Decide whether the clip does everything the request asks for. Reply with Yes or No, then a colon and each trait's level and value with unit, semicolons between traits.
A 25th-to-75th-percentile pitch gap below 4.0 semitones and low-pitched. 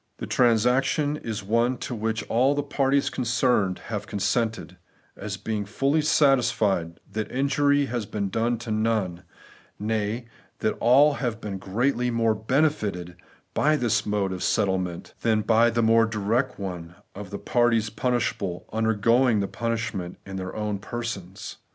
Yes: average, 3.4 semitones; low, 115 Hz